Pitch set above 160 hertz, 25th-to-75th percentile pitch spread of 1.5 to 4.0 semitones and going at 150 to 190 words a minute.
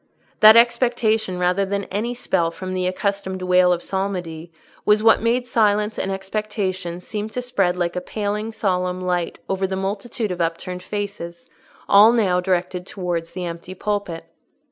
Yes: high, 190 Hz; average, 2.8 semitones; average, 160 wpm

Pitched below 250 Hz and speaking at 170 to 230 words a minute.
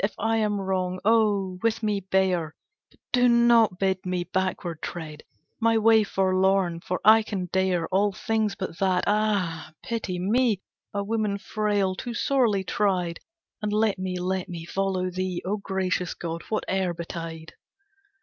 No: high, 190 Hz; average, 155 wpm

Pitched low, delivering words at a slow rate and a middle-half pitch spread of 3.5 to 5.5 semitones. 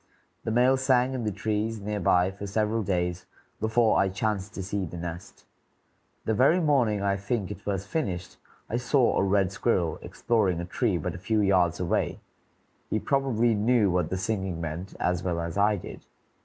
No: low, 100 Hz; average, 185 wpm; average, 3.8 semitones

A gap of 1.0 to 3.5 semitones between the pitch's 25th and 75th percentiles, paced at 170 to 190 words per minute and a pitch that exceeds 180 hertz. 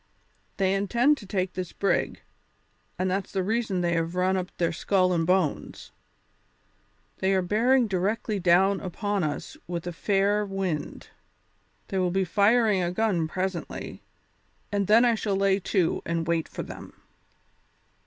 No: narrow, 2.5 semitones; average, 155 wpm; high, 190 Hz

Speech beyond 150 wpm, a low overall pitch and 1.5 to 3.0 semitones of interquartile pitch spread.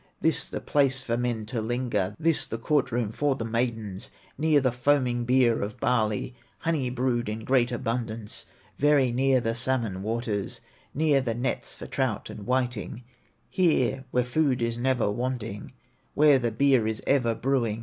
Yes: average, 165 wpm; low, 125 Hz; narrow, 2.6 semitones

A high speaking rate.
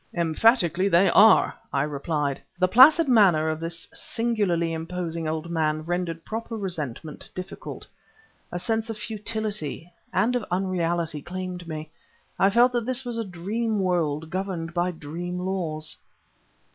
No: average, 140 wpm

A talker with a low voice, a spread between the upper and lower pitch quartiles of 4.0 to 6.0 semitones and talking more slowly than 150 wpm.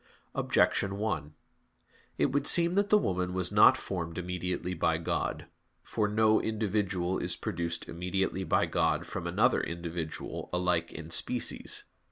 No: very low, 90 Hz; average, 3.6 semitones; average, 140 wpm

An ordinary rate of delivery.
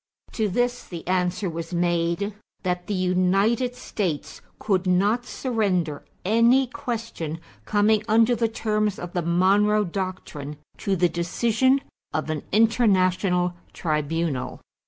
No: slow, 120 wpm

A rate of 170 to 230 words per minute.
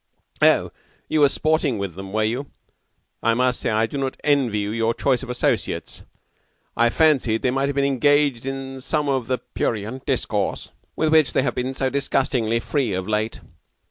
Yes: average, 185 wpm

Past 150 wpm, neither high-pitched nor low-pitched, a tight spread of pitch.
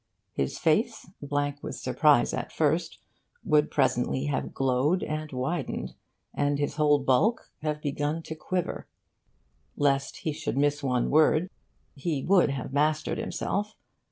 No: slow, 135 wpm; medium, 145 Hz; narrow, 2.3 semitones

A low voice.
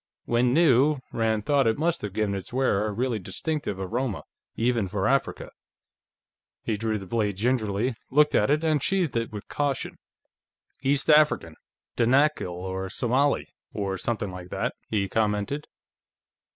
Yes: low, 115 Hz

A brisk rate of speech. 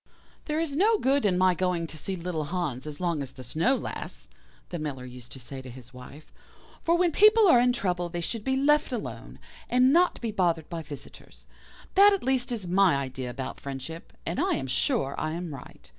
Yes: fast, 215 wpm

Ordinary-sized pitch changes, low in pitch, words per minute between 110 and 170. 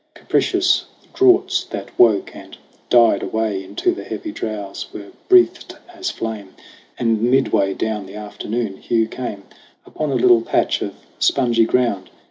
Yes: average, 3.5 semitones; low, 115 Hz; average, 140 wpm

